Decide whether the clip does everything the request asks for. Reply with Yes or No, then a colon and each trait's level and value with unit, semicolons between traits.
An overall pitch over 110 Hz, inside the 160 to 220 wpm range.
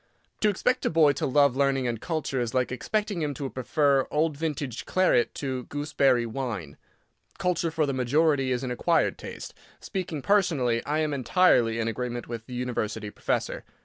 Yes: low, 135 Hz; average, 175 wpm